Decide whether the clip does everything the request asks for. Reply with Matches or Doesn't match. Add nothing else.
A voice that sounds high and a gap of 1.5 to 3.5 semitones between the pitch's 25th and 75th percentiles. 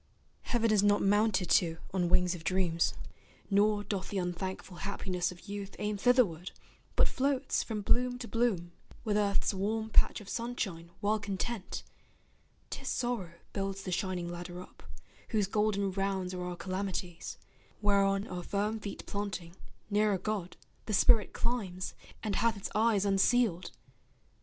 Matches